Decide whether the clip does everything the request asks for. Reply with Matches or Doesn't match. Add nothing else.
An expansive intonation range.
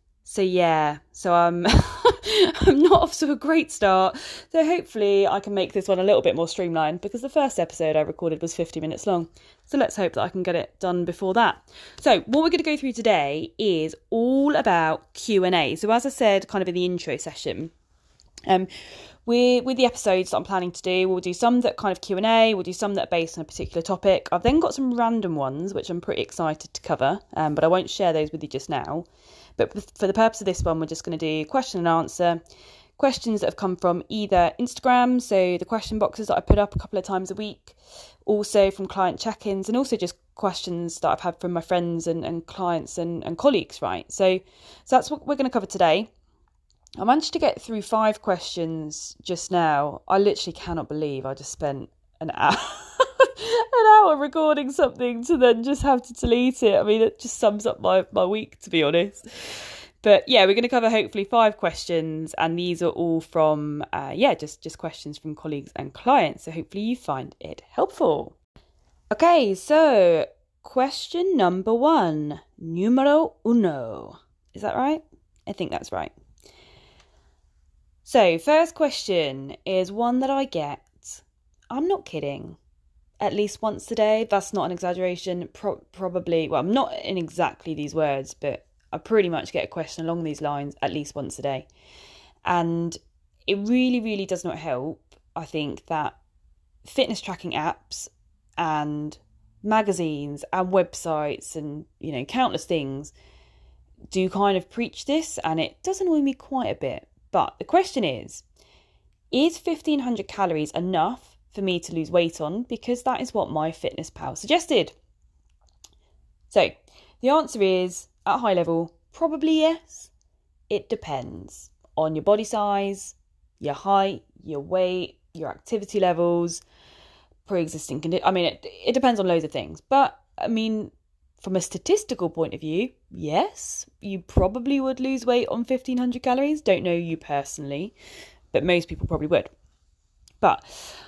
Matches